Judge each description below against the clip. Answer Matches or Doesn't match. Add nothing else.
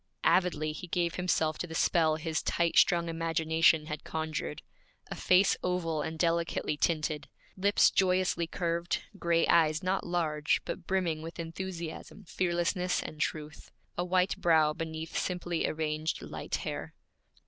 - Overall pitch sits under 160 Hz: Doesn't match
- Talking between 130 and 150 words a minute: Matches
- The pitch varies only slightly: Matches